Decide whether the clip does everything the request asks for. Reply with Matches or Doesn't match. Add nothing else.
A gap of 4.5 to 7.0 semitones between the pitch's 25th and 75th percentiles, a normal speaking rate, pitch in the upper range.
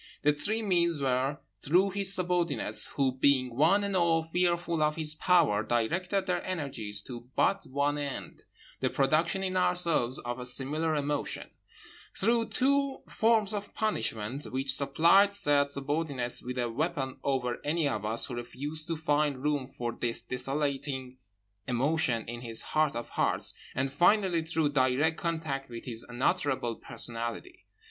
Doesn't match